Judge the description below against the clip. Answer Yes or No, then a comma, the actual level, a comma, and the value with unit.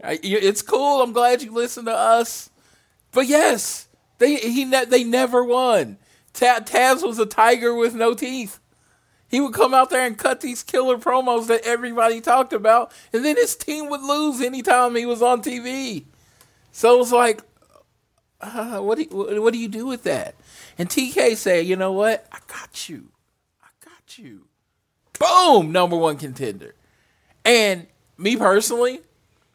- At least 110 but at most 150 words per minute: No, average, 160 wpm